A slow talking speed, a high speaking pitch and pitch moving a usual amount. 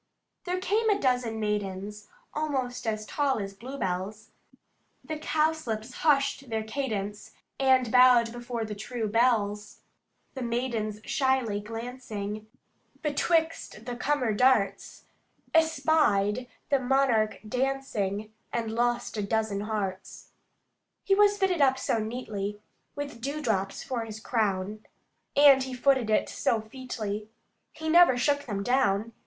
Yes: slow, 125 wpm; high, 240 Hz; average, 4.2 semitones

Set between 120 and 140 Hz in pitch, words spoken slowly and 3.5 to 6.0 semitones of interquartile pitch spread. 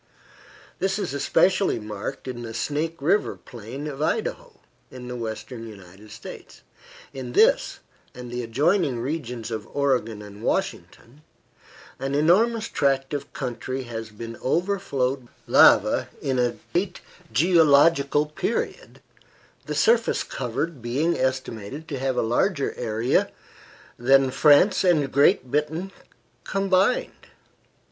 Yes: low, 135 Hz; slow, 120 wpm; wide, 5.5 semitones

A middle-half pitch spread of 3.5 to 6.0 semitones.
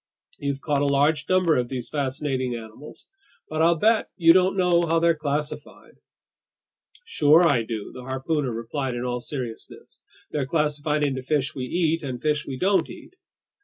Yes: average, 3.8 semitones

